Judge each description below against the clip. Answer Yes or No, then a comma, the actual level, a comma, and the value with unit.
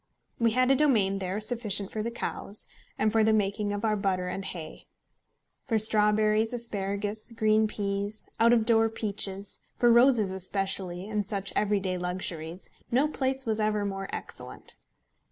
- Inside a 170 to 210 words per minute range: No, average, 155 wpm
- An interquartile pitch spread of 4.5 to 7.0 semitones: No, narrow, 2.4 semitones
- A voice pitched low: No, high, 210 Hz